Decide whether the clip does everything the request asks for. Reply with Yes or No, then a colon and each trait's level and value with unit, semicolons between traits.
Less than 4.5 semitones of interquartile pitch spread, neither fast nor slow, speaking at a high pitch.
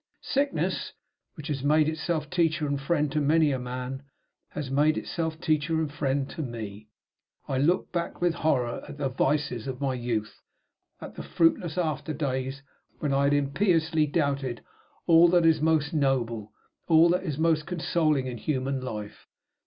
No: average, 3.3 semitones; average, 165 wpm; medium, 145 Hz